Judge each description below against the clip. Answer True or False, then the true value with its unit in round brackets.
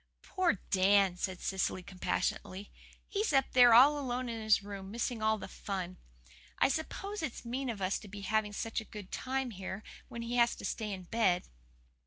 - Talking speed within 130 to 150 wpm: False (190 wpm)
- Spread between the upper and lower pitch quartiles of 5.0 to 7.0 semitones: False (4.2 semitones)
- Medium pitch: False (220 Hz)